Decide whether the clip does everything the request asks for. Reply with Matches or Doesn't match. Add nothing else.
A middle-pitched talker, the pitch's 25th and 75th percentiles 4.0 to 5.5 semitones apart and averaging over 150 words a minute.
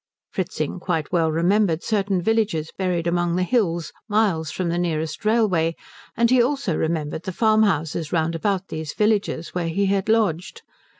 Matches